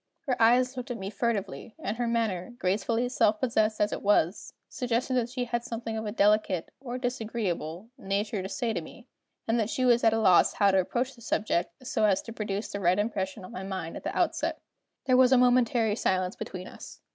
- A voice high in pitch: Yes, high, 220 Hz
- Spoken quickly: Yes, fast, 215 wpm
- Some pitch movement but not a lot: Yes, average, 3.7 semitones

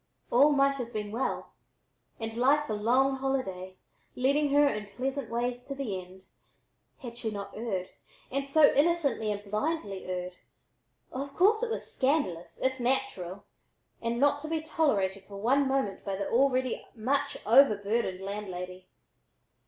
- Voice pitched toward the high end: Yes, high, 240 Hz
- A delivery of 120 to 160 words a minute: Yes, average, 150 wpm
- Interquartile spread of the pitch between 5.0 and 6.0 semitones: Yes, wide, 5.5 semitones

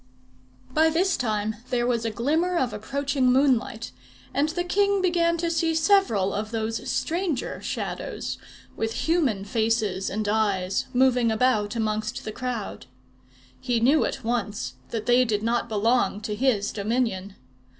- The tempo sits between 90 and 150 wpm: Yes, average, 145 wpm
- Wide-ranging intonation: No, average, 4.8 semitones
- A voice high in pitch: Yes, high, 235 Hz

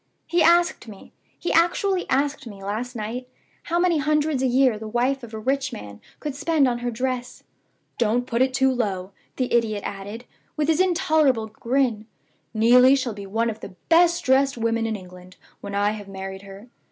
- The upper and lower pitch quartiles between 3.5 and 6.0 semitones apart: Yes, average, 4.4 semitones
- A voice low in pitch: No, high, 245 Hz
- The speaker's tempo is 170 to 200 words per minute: Yes, average, 190 wpm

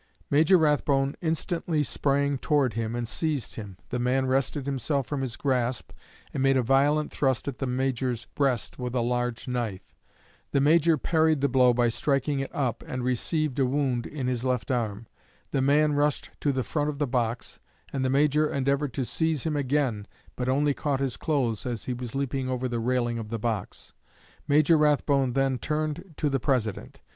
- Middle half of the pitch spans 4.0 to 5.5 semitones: No, average, 3.0 semitones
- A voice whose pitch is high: No, low, 135 Hz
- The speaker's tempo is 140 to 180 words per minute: No, average, 190 wpm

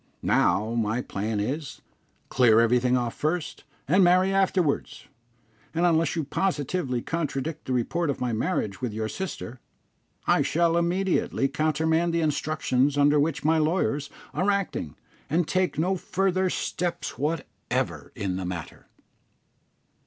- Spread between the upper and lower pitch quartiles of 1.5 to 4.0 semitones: No, wide, 5.6 semitones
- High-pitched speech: No, medium, 155 Hz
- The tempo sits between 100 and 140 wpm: Yes, slow, 135 wpm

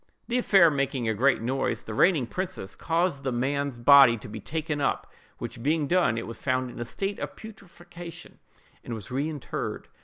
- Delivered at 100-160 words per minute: No, average, 185 wpm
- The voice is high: No, medium, 140 Hz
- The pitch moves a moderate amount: No, wide, 6.0 semitones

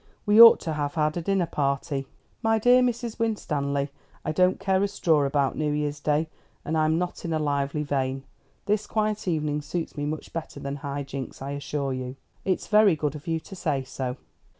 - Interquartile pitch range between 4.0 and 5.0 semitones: Yes, average, 4.7 semitones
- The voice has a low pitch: No, medium, 150 Hz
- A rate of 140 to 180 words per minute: No, fast, 205 wpm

